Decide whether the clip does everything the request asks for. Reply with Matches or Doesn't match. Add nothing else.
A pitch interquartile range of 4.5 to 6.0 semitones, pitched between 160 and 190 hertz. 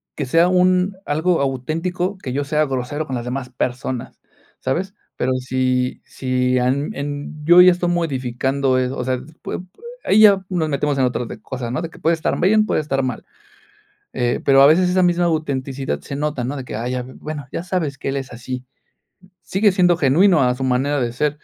Doesn't match